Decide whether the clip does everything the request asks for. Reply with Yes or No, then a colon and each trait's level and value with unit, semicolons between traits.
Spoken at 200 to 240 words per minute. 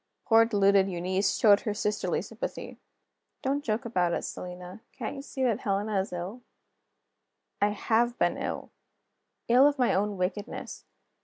No: average, 150 wpm